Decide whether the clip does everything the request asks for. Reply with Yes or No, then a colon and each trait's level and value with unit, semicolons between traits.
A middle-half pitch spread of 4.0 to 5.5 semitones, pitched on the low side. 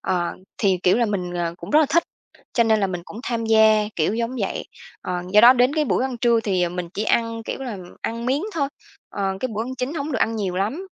No: average, 4.7 semitones; high, 225 Hz